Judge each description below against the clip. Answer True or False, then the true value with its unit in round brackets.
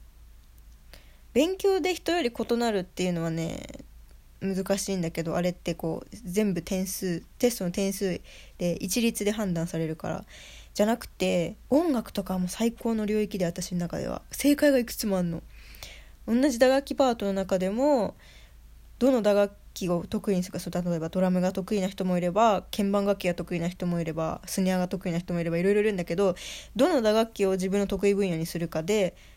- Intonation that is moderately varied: True (3.6 semitones)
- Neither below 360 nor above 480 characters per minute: True (365 characters per minute)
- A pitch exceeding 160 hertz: True (190 Hz)